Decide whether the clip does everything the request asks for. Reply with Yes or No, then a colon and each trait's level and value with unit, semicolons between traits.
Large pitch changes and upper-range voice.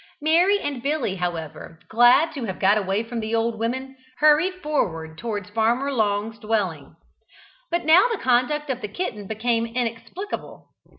Yes: wide, 5.9 semitones; high, 230 Hz